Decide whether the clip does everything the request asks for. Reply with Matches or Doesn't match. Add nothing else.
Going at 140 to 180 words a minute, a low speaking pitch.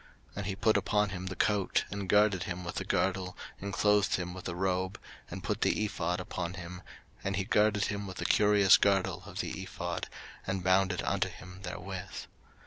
Doesn't match